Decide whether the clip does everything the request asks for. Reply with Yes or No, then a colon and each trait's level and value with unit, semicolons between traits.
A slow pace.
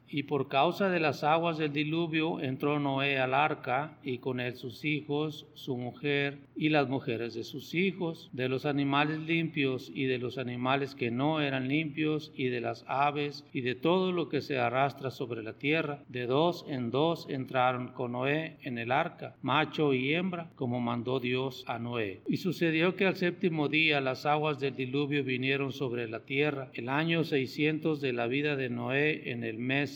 No: fast, 190 wpm